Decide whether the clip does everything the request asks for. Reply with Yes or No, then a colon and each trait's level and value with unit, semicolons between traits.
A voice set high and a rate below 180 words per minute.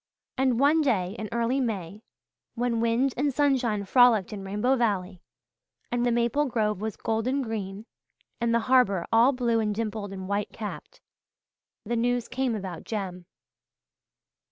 Yes: high, 230 Hz; average, 150 wpm